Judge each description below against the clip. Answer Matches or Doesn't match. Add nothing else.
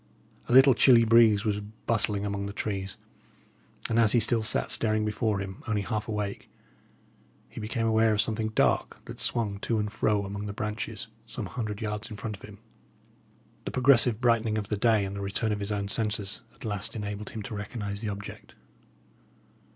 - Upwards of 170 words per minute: Matches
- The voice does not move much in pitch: Matches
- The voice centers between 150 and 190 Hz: Doesn't match